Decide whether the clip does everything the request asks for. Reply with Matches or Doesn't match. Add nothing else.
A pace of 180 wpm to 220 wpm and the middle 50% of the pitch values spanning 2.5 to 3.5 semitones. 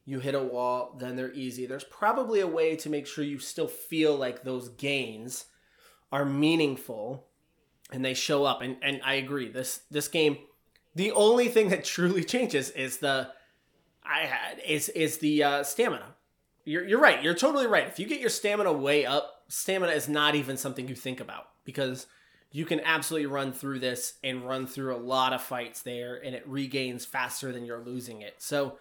Matches